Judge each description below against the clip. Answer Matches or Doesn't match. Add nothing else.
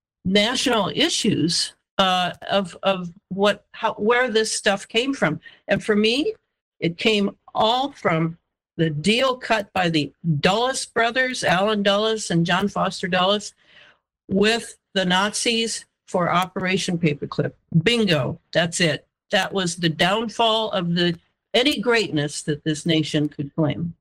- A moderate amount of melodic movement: Matches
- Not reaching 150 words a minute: Matches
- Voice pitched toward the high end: Matches